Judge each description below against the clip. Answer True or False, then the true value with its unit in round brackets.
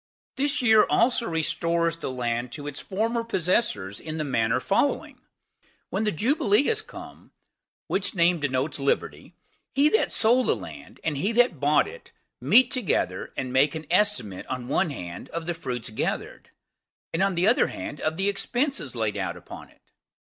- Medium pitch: True (170 Hz)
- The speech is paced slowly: False (170 wpm)